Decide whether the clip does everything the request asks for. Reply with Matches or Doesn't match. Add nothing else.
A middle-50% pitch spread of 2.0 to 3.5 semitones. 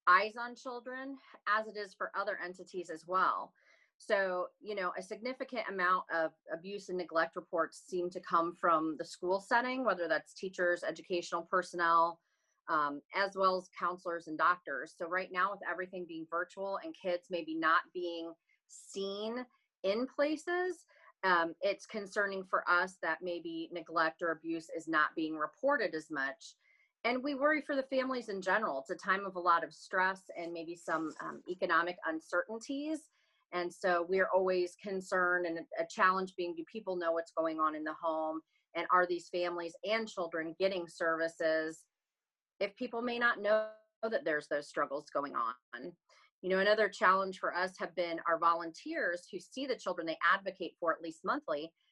Matches